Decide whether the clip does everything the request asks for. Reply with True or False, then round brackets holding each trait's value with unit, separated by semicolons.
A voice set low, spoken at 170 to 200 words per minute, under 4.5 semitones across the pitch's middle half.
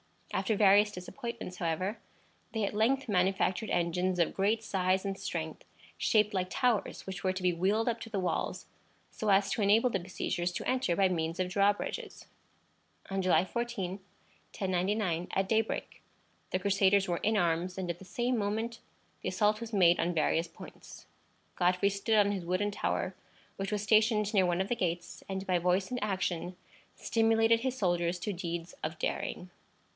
False (195 Hz; 175 wpm; 3.0 semitones)